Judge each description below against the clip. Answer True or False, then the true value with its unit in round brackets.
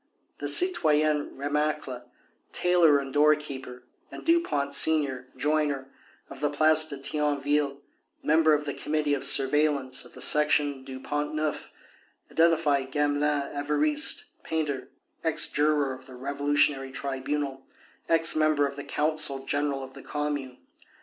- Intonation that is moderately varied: False (1.8 semitones)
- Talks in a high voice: False (145 Hz)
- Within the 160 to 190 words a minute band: False (135 wpm)